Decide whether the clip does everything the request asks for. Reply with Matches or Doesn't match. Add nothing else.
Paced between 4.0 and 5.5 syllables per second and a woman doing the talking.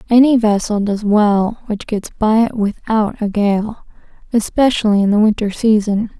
Matches